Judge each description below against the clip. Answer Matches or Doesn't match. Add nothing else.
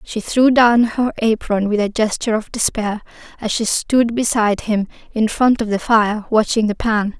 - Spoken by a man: Doesn't match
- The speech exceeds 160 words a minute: Matches